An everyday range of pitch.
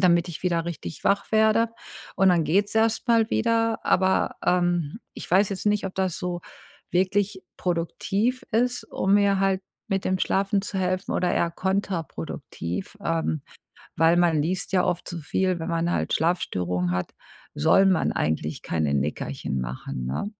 Yes: average, 3.2 semitones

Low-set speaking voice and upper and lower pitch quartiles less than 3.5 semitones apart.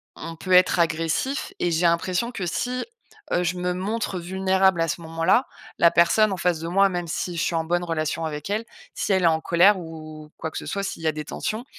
No: medium, 175 Hz; narrow, 2.6 semitones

